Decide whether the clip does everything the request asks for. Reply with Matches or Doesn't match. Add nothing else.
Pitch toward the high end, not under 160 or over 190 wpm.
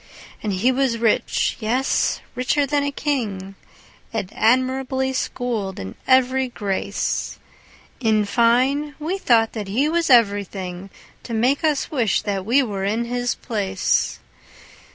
Doesn't match